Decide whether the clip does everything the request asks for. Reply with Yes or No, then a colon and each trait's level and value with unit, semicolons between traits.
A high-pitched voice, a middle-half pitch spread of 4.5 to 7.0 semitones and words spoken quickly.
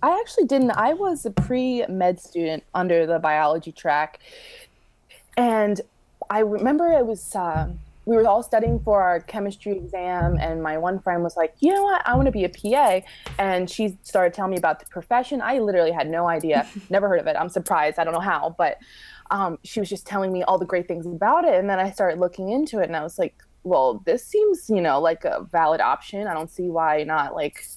Yes: high, 195 Hz; wide, 5.6 semitones; fast, 225 wpm